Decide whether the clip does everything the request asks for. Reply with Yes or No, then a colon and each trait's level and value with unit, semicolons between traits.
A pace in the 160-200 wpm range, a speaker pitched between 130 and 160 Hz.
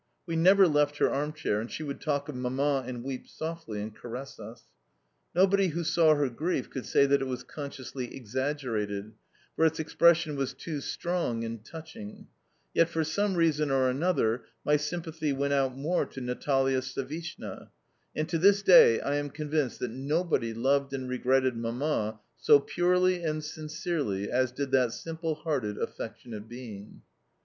Yes: average, 165 wpm; medium, 140 Hz